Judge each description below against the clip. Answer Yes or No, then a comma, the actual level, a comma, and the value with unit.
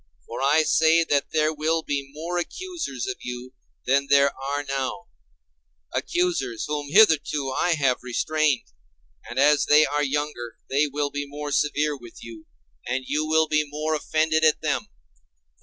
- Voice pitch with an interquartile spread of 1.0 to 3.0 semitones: Yes, narrow, 2.5 semitones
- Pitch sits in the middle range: Yes, medium, 145 Hz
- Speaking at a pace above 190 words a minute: No, average, 155 wpm